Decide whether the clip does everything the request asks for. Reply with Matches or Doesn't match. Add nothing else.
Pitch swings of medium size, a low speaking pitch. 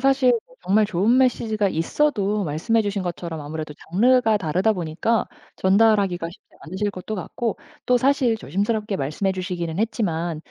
Doesn't match